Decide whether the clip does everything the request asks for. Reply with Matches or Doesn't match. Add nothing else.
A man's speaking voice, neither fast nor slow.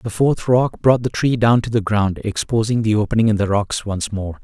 Doesn't match